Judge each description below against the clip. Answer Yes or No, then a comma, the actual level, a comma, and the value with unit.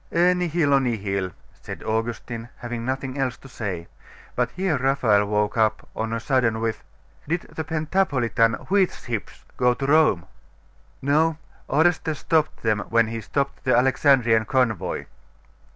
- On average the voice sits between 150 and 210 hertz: No, low, 125 Hz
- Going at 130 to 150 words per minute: Yes, average, 140 wpm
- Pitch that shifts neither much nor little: Yes, average, 4.6 semitones